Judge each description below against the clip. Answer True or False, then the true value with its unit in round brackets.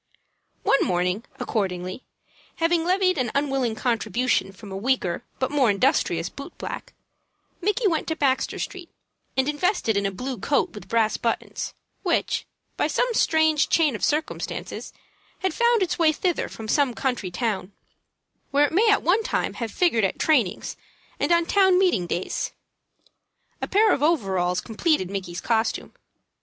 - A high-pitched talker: True (265 Hz)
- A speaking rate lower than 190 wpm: True (155 wpm)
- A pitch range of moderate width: False (8.3 semitones)